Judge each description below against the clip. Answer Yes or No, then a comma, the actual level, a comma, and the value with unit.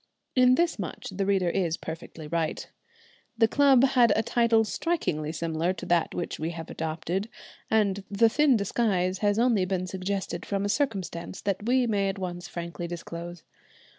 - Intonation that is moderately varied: Yes, average, 4.6 semitones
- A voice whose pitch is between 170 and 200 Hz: Yes, high, 190 Hz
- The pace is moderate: Yes, average, 165 wpm